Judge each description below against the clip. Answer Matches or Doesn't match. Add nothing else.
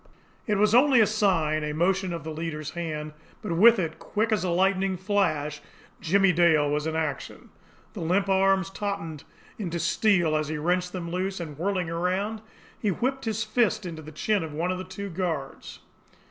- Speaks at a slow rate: Doesn't match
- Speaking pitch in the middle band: Matches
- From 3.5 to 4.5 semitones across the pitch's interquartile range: Matches